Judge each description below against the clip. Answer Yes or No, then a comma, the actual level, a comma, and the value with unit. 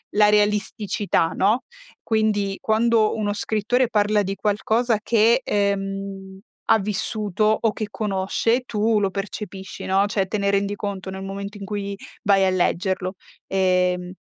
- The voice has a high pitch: Yes, high, 205 Hz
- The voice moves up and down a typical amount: No, narrow, 1.8 semitones